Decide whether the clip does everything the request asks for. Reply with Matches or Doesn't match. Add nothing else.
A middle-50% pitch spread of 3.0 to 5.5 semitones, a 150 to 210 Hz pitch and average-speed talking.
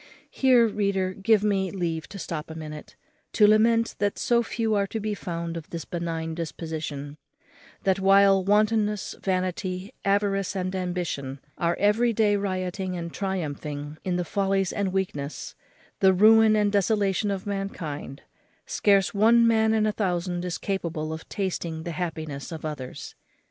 Matches